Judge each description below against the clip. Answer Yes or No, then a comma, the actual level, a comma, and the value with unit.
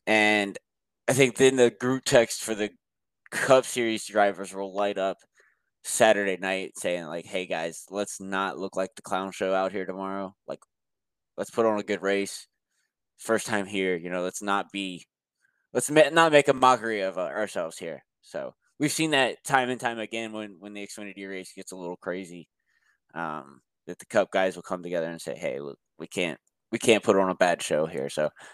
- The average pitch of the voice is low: Yes, low, 100 Hz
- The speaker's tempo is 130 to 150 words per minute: No, average, 200 wpm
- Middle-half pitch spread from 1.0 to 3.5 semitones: Yes, average, 3.1 semitones